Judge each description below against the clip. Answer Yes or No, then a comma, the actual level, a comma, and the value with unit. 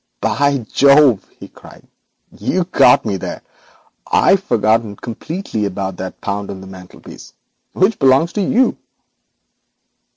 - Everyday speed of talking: No, slow, 125 wpm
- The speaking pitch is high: No, low, 120 Hz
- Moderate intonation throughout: No, wide, 8.9 semitones